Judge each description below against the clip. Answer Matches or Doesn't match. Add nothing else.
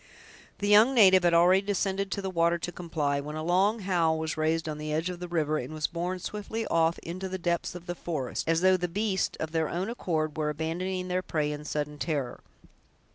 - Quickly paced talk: Matches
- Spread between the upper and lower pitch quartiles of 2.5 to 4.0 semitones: Matches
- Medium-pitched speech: Matches